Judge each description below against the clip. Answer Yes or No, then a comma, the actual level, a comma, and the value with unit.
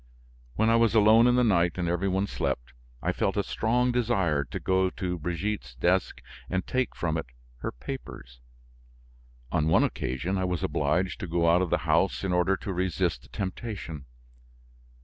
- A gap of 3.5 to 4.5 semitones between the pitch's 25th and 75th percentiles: Yes, average, 4.0 semitones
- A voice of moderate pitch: No, very low, 90 Hz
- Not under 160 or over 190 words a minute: Yes, average, 180 wpm